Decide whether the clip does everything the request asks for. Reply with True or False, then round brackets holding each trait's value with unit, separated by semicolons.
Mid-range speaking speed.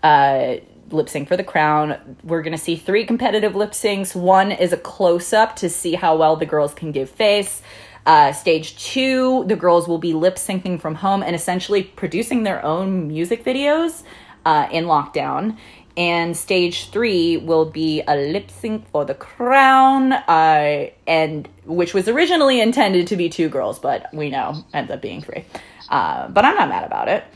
True (180 wpm)